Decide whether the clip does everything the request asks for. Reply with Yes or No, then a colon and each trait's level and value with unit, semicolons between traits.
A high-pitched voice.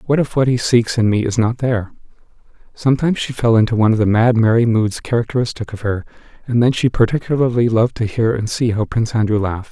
No: low, 115 Hz